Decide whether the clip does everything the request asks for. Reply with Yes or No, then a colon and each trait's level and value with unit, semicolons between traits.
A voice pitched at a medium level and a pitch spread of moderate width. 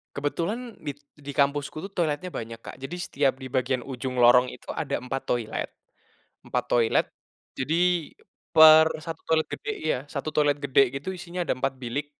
Yes: medium, 145 Hz; average, 3.7 semitones